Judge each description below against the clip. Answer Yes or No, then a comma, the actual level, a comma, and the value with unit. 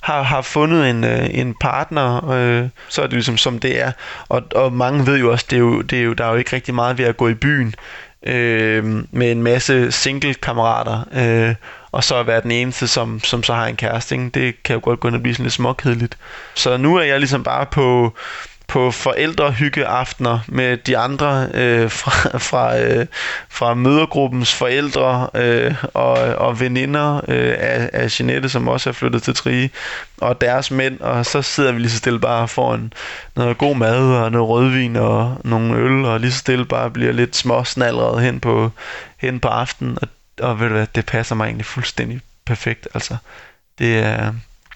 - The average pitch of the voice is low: Yes, low, 120 Hz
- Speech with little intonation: Yes, narrow, 2.3 semitones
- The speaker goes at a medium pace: Yes, average, 200 wpm